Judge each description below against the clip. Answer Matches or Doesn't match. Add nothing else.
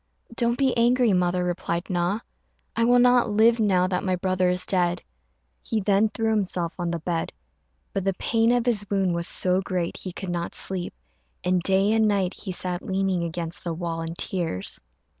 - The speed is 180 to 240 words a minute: Matches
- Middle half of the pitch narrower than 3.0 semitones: Doesn't match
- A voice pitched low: Doesn't match